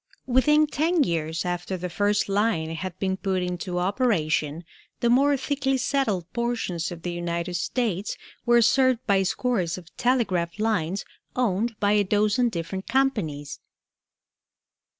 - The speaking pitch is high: Yes, high, 200 Hz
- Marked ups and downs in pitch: Yes, wide, 5.7 semitones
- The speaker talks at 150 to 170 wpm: No, slow, 135 wpm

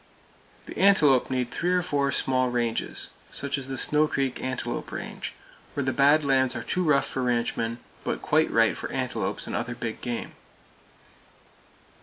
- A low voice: Yes, low, 130 Hz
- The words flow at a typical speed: Yes, average, 165 wpm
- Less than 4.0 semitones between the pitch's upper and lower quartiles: Yes, average, 2.8 semitones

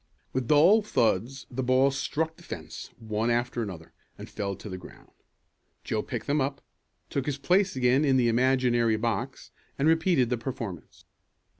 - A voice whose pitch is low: Yes, low, 130 Hz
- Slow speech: No, average, 170 wpm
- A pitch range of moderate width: Yes, average, 3.4 semitones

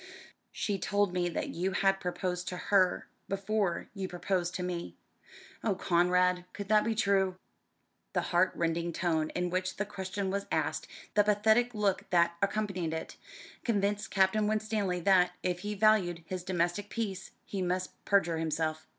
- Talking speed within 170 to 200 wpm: No, average, 160 wpm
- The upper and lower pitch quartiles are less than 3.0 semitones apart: Yes, narrow, 2.4 semitones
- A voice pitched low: No, medium, 185 Hz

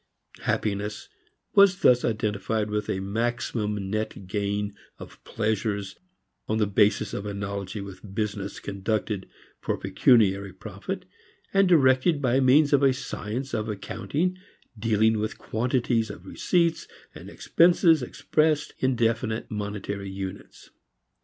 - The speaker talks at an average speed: No, slow, 120 wpm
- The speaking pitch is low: Yes, low, 110 Hz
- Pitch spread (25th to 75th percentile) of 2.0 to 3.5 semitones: No, average, 4.2 semitones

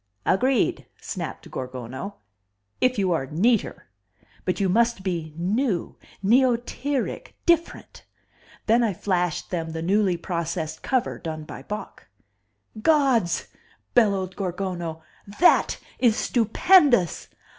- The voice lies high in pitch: Yes, high, 195 Hz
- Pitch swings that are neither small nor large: No, wide, 6.0 semitones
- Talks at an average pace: No, slow, 105 wpm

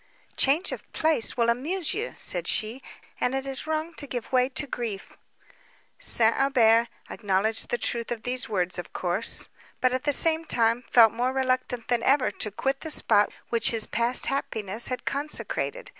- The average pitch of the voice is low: No, high, 245 Hz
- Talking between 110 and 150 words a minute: No, average, 175 wpm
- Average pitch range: Yes, average, 3.4 semitones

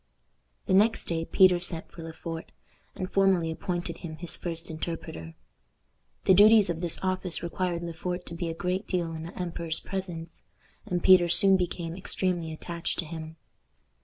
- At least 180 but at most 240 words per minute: No, average, 170 wpm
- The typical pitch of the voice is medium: Yes, medium, 175 Hz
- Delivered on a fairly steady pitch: Yes, narrow, 2.0 semitones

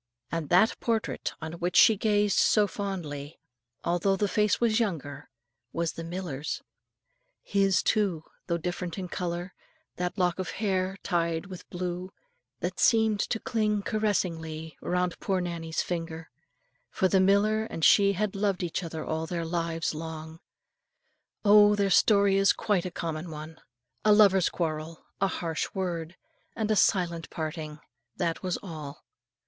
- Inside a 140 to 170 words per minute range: Yes, average, 150 wpm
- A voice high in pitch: No, medium, 180 Hz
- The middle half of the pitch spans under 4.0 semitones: Yes, average, 3.5 semitones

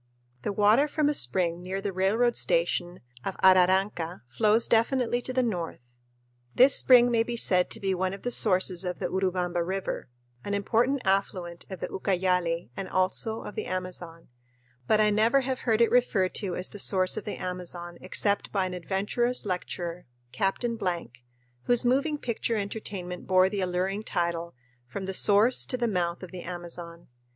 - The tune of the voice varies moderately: Yes, average, 4.0 semitones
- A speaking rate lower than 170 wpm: No, average, 175 wpm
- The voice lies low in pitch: No, high, 190 Hz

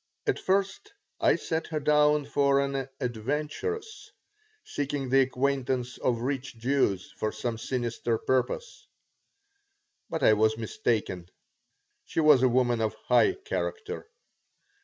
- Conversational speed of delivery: No, slow, 120 wpm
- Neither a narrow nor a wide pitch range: Yes, average, 3.9 semitones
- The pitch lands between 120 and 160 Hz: Yes, low, 135 Hz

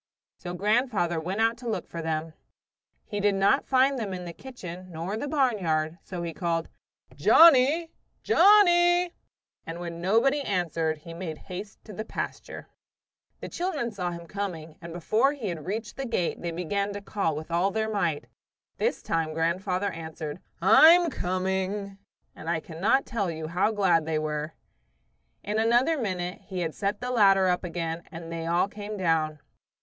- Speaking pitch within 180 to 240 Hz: Yes, medium, 185 Hz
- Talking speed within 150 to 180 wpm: Yes, average, 170 wpm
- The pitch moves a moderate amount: Yes, average, 4.9 semitones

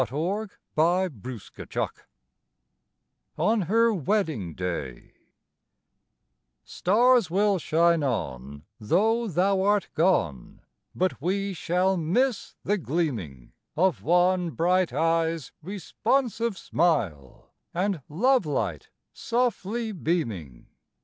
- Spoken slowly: Yes, slow, 90 wpm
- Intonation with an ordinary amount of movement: No, wide, 6.7 semitones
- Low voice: No, medium, 175 Hz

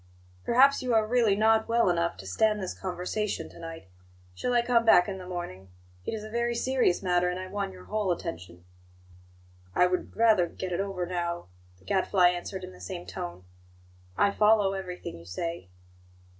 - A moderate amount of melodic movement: Yes, average, 4.0 semitones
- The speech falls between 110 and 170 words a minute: No, average, 185 wpm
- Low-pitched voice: No, medium, 185 Hz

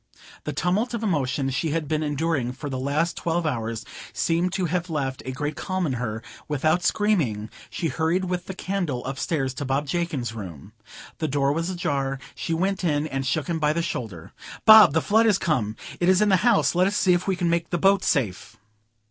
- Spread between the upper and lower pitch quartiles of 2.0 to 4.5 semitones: No, average, 5.1 semitones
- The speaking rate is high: Yes, fast, 210 wpm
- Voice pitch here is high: No, medium, 160 Hz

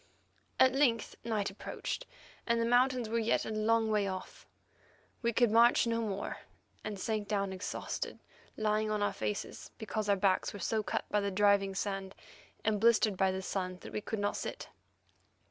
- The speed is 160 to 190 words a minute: Yes, average, 180 wpm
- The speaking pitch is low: No, high, 215 Hz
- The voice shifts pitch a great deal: No, narrow, 2.4 semitones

